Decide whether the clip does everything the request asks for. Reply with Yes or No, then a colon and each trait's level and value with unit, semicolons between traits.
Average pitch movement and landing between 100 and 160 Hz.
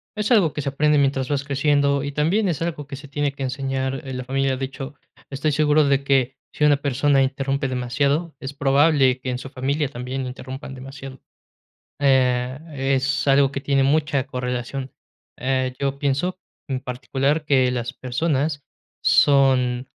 No: narrow, 1.6 semitones; low, 135 Hz